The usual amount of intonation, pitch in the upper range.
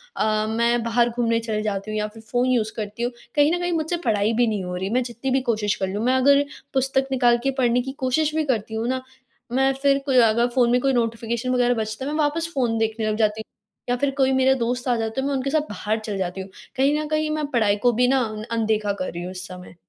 Yes: average, 3.5 semitones; high, 235 Hz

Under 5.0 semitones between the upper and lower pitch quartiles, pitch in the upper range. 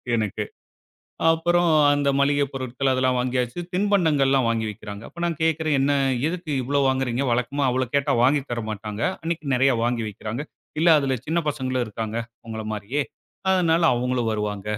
No: average, 4.0 semitones; low, 130 Hz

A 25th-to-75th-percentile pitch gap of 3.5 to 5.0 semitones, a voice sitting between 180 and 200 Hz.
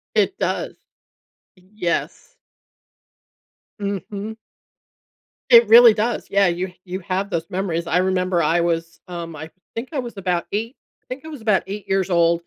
Yes: average, 3.9 semitones; high, 190 Hz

